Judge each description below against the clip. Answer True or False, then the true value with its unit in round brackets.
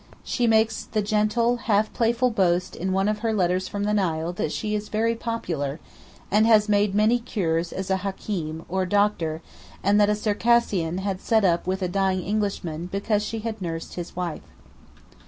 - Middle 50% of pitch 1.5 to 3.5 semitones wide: True (3.2 semitones)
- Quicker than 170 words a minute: True (185 wpm)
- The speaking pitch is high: True (200 Hz)